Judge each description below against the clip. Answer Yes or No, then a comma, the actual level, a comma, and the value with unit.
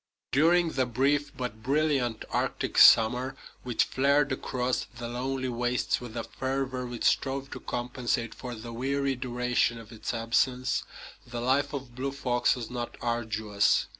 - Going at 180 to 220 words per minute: No, average, 150 wpm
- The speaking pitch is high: No, low, 125 Hz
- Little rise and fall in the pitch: Yes, narrow, 2.1 semitones